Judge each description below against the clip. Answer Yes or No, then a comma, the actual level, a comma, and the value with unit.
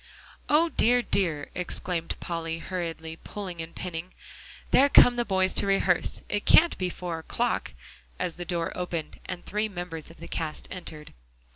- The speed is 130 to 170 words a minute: Yes, average, 160 wpm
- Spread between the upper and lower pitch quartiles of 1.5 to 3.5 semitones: Yes, average, 3.1 semitones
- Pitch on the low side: No, medium, 175 Hz